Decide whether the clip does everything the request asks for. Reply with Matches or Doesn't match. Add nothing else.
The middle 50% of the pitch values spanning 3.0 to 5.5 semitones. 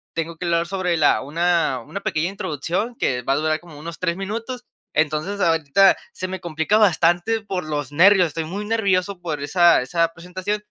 Matches